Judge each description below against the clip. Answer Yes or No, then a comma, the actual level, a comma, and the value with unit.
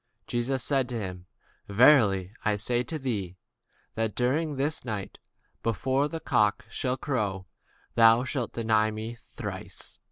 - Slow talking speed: Yes, slow, 125 wpm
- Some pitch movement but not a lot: Yes, average, 3.9 semitones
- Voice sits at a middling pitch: No, low, 115 Hz